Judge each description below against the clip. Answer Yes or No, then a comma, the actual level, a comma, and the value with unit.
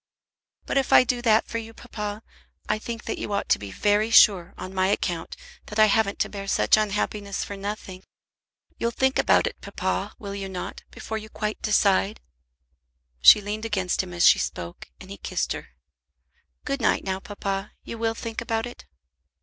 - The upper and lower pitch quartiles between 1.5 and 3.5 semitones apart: Yes, narrow, 2.5 semitones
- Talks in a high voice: Yes, high, 210 Hz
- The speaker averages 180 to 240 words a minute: Yes, average, 190 wpm